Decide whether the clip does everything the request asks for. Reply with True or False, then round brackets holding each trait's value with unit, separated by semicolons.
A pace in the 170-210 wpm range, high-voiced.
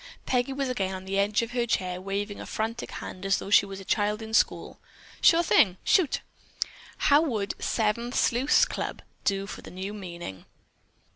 True (185 wpm; 210 Hz)